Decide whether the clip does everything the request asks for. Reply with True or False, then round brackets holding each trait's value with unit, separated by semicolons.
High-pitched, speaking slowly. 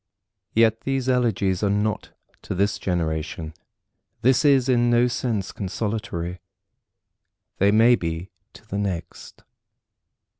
False (105 Hz; 115 wpm)